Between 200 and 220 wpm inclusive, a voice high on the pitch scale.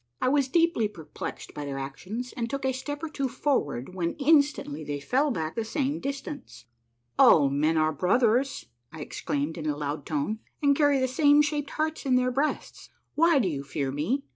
Yes: fast, 205 wpm; high, 240 Hz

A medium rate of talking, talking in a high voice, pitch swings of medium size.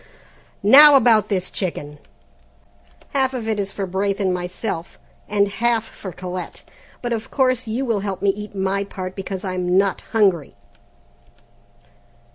Yes: average, 145 wpm; high, 200 Hz; average, 3.2 semitones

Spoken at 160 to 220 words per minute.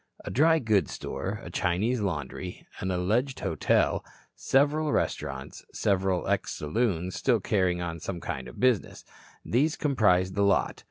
No: average, 145 wpm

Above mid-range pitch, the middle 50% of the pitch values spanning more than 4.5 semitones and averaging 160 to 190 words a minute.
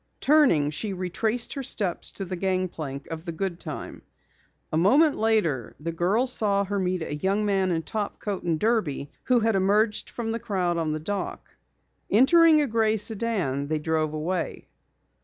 Yes: high, 195 Hz; average, 5.1 semitones; average, 165 wpm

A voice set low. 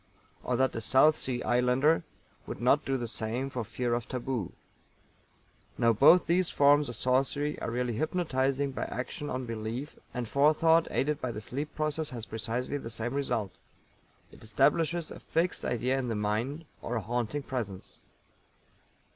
Yes: low, 130 Hz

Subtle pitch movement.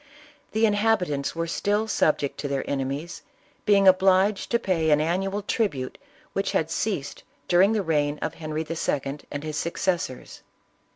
No: average, 5.1 semitones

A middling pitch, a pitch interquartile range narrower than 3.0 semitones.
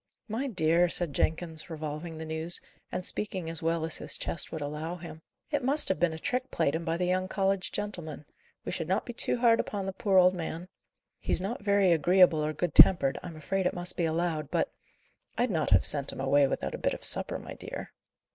No: medium, 170 Hz; average, 3.3 semitones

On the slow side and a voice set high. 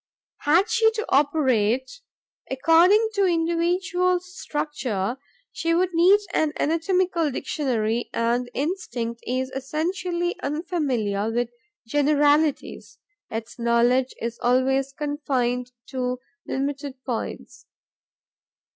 Yes: slow, 95 wpm; very high, 285 Hz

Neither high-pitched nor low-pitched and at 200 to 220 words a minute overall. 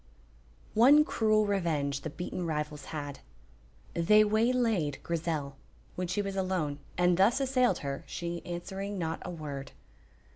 No: medium, 175 Hz; slow, 135 wpm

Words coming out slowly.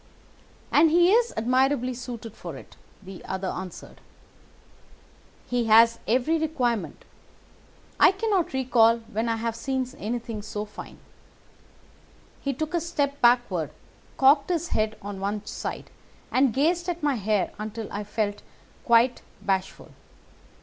Yes: slow, 130 wpm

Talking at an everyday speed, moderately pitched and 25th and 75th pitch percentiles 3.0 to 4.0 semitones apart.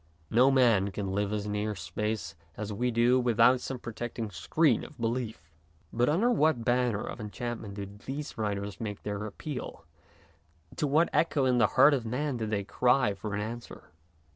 No: average, 175 wpm; low, 115 Hz; average, 3.6 semitones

